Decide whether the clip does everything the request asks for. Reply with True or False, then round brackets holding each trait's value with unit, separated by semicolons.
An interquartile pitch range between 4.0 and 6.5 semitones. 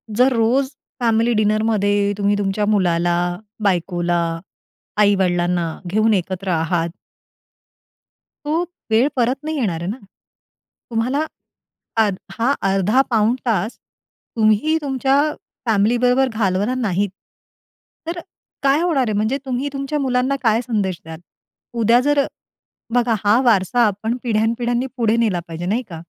True (4.3 semitones)